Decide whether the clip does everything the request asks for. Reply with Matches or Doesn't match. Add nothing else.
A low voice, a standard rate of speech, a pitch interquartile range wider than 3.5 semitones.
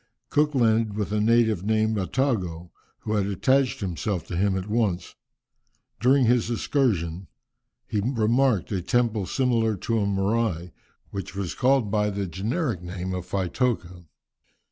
Matches